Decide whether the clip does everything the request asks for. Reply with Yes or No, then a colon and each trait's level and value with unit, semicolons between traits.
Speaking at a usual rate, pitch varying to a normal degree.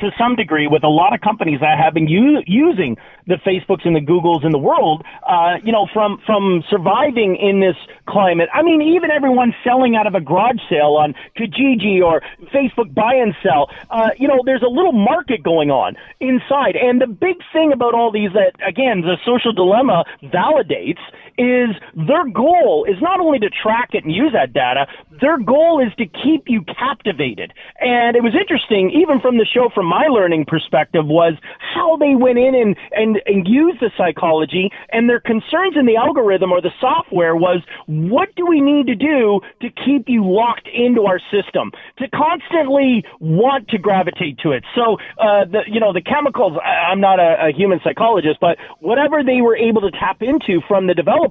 No: average, 195 wpm; wide, 6.2 semitones